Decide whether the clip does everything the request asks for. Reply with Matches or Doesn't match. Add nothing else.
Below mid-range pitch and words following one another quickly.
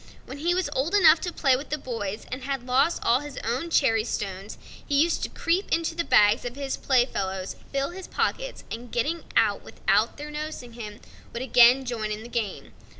Doesn't match